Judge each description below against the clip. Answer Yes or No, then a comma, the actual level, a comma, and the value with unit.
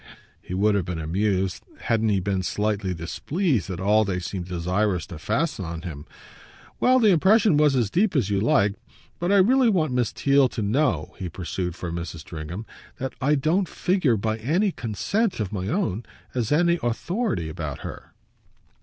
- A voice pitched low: Yes, low, 110 Hz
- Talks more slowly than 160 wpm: No, average, 180 wpm